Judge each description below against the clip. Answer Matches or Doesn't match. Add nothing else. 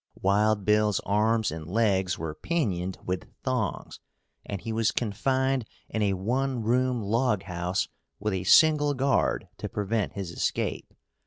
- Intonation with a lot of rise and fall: Doesn't match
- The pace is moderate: Matches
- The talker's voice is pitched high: Doesn't match